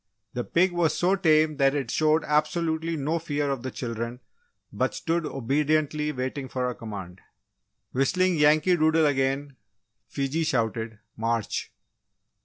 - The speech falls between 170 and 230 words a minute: No, slow, 135 wpm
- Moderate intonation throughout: Yes, average, 3.6 semitones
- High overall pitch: No, medium, 145 Hz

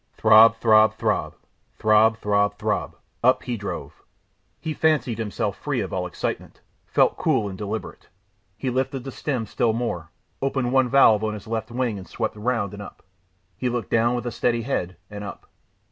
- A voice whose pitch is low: Yes, low, 115 Hz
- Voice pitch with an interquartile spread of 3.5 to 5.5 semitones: No, average, 2.8 semitones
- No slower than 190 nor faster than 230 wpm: No, average, 175 wpm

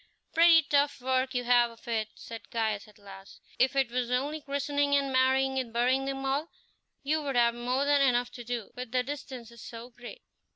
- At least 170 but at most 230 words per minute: Yes, average, 200 wpm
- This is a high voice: Yes, very high, 255 Hz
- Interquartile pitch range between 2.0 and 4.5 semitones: Yes, average, 2.7 semitones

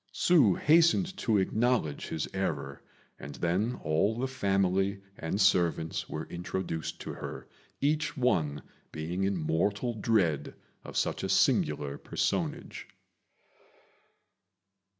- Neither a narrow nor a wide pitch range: No, wide, 6.8 semitones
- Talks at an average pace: No, slow, 110 wpm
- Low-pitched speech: Yes, very low, 95 Hz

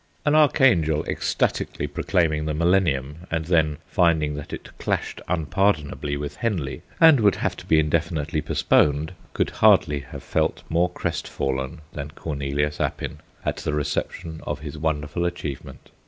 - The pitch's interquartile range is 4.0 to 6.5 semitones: No, average, 2.9 semitones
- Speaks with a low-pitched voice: Yes, very low, 80 Hz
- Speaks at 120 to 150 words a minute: Yes, average, 140 wpm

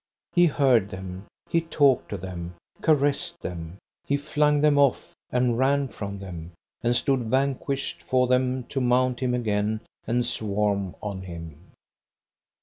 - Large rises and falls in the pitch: Yes, wide, 6.1 semitones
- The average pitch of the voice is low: Yes, low, 120 Hz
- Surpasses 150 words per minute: No, average, 145 wpm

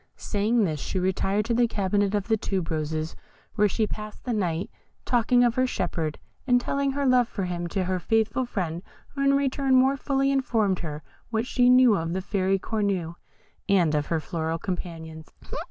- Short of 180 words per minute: No, average, 185 wpm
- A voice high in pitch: Yes, high, 205 Hz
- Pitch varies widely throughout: Yes, wide, 6.0 semitones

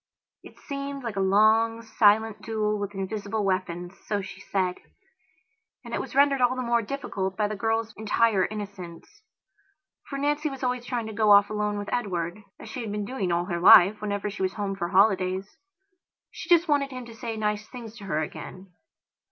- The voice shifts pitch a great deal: No, average, 3.2 semitones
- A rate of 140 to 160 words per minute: No, average, 190 wpm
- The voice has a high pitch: Yes, high, 210 Hz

